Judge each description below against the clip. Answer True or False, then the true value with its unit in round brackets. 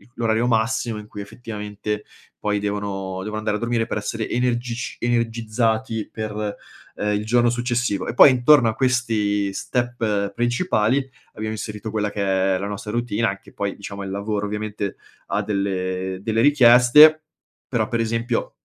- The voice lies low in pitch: True (110 Hz)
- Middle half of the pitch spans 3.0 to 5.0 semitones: False (2.6 semitones)